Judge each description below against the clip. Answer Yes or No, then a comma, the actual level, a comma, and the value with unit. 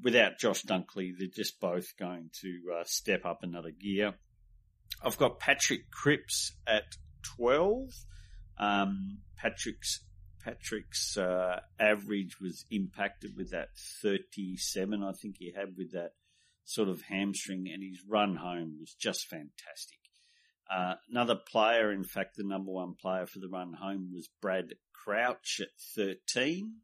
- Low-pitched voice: Yes, very low, 95 Hz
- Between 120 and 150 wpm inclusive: Yes, average, 140 wpm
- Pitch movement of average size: No, narrow, 2.2 semitones